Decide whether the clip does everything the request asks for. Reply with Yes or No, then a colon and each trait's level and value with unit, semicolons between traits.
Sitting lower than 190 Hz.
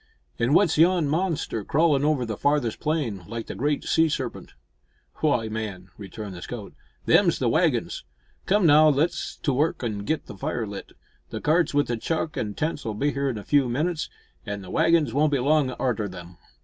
Yes: medium, 140 Hz